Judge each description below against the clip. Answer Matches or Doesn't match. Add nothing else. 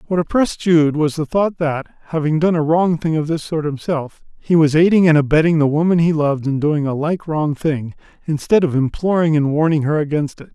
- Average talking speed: Doesn't match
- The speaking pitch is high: Doesn't match